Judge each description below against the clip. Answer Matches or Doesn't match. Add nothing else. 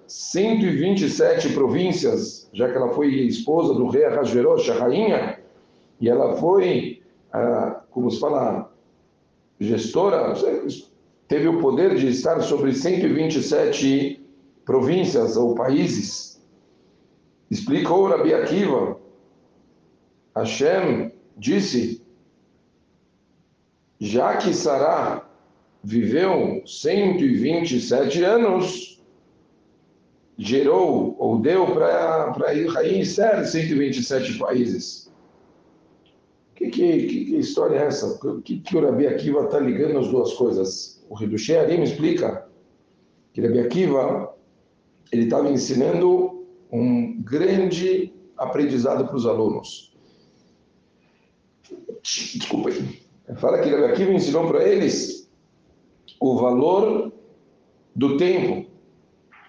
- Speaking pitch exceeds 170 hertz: Matches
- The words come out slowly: Matches